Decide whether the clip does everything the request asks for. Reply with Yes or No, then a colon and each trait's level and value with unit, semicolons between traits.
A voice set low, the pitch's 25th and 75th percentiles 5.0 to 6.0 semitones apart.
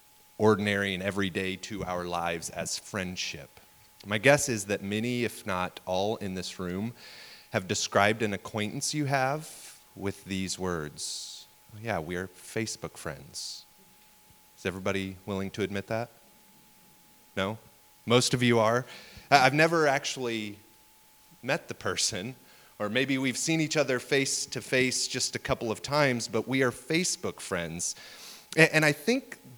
Yes: low, 110 Hz; wide, 5.4 semitones